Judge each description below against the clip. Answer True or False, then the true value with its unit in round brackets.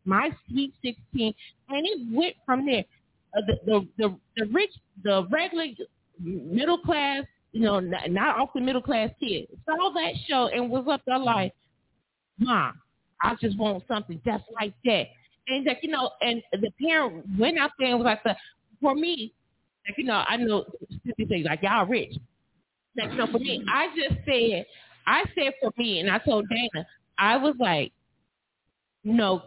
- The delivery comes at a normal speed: True (175 wpm)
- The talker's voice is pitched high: True (240 Hz)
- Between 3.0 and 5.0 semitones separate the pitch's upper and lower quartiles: True (4.7 semitones)